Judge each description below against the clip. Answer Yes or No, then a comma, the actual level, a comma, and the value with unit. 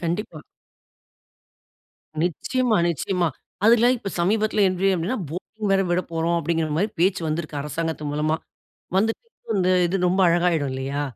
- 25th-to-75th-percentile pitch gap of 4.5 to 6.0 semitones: No, average, 3.7 semitones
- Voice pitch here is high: No, medium, 175 Hz